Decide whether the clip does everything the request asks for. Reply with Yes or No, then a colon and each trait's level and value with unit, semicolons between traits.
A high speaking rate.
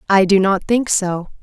Yes: fast, 210 wpm